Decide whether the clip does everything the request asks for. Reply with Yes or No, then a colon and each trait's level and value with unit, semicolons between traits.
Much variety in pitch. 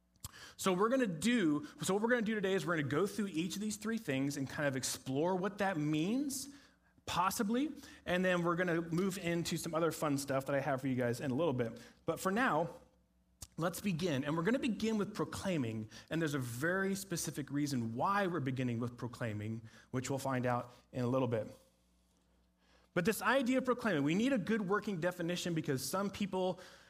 Yes: wide, 7.4 semitones